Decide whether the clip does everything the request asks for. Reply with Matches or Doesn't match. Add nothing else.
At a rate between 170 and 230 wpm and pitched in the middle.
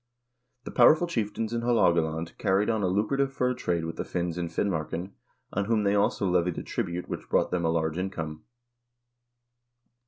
Doesn't match